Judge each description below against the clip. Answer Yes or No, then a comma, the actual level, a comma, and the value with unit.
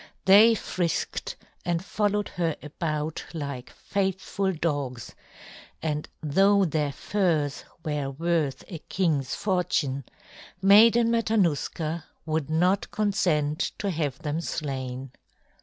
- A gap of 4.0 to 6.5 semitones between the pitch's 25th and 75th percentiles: Yes, average, 4.7 semitones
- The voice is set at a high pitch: No, medium, 165 Hz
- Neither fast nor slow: No, slow, 105 wpm